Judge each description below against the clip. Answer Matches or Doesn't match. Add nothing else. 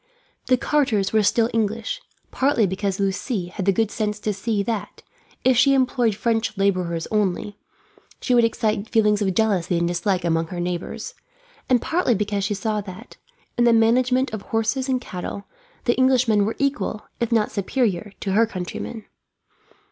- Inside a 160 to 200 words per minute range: Matches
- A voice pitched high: Matches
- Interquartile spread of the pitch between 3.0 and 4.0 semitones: Matches